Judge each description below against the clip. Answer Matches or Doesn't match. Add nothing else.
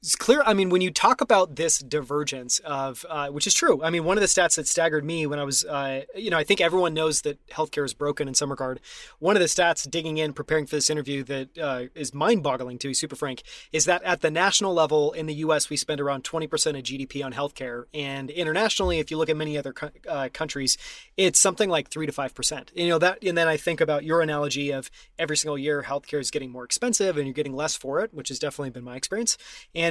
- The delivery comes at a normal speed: Doesn't match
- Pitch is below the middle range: Doesn't match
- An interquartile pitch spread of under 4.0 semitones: Matches